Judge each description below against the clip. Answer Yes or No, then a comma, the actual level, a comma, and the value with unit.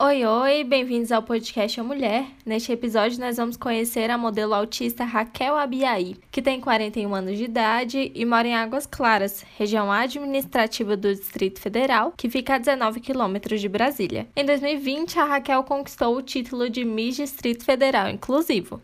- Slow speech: No, average, 165 wpm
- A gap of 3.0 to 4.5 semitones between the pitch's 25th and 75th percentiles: Yes, average, 3.5 semitones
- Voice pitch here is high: Yes, high, 240 Hz